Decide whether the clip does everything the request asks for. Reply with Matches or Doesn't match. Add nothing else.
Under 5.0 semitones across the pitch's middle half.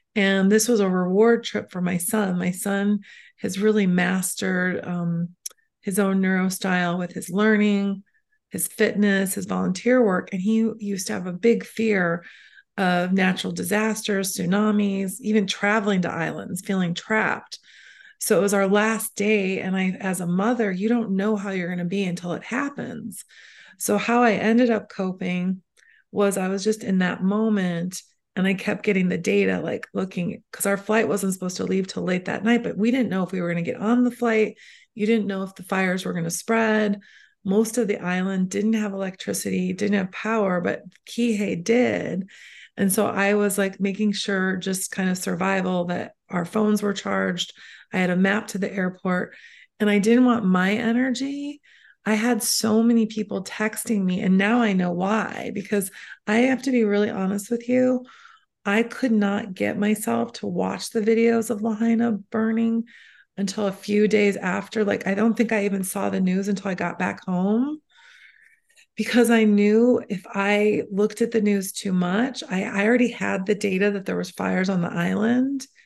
Matches